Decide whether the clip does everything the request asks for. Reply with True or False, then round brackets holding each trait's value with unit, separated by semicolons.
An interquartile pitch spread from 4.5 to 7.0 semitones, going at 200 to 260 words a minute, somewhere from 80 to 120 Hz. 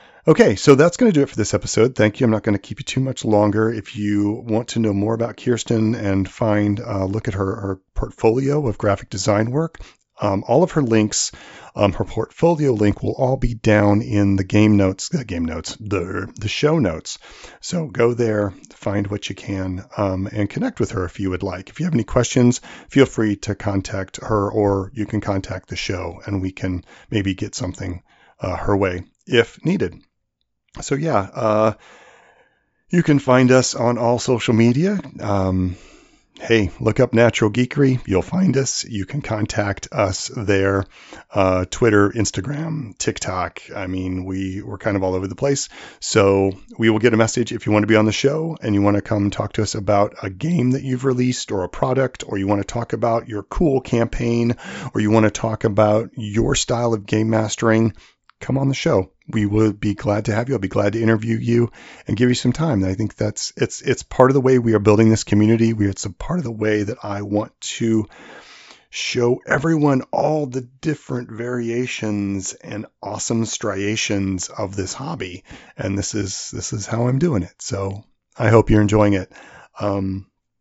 False (3.4 semitones; 205 wpm; 110 Hz)